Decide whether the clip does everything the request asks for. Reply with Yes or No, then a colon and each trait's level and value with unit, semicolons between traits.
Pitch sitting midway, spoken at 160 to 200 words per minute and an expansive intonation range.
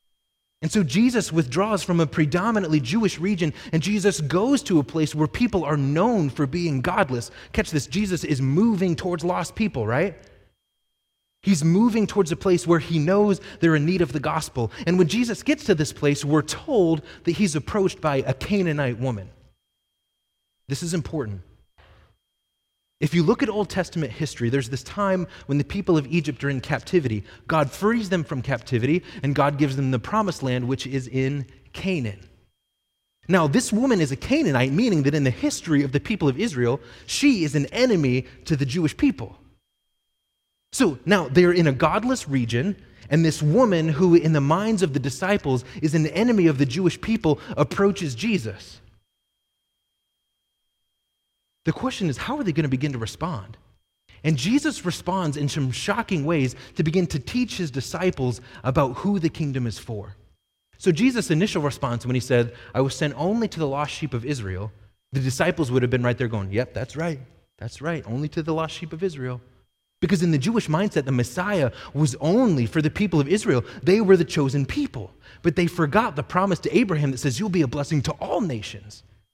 Yes: medium, 155 Hz; average, 190 wpm; wide, 5.9 semitones